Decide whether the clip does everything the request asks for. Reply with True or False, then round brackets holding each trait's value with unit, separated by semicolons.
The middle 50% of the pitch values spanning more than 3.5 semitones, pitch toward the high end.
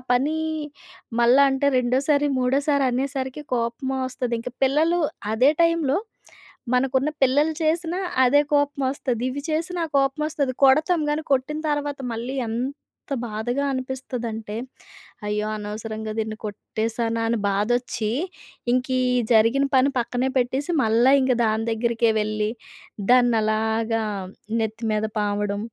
True (3.9 semitones; 255 Hz)